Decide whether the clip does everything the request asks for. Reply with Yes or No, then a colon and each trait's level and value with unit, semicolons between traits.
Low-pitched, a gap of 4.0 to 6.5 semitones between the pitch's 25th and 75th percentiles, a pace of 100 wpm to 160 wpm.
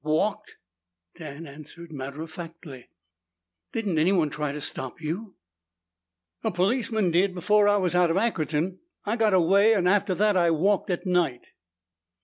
No: medium, 180 Hz; average, 4.4 semitones; average, 150 wpm